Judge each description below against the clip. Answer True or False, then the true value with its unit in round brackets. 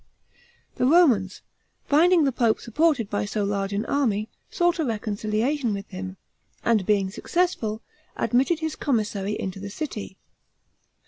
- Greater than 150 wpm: False (135 wpm)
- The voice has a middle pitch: False (220 Hz)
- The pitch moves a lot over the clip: True (6.3 semitones)